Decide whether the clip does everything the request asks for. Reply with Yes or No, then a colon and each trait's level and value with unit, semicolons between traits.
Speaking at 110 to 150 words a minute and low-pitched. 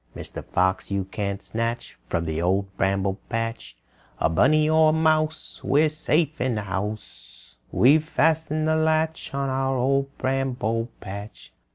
Yes: average, 145 wpm; low, 125 Hz